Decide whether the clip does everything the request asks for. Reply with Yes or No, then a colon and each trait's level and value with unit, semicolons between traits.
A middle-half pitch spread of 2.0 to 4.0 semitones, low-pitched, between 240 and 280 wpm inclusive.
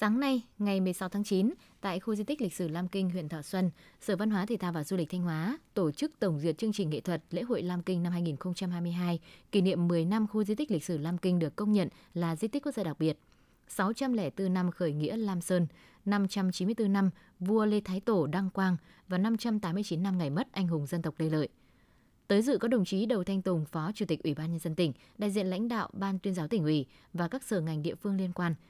No: average, 3.4 semitones; medium, 185 Hz; fast, 250 wpm